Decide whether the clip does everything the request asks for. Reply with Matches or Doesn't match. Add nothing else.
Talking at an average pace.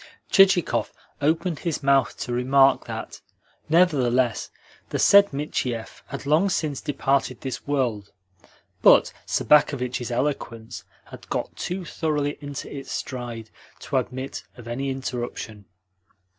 Doesn't match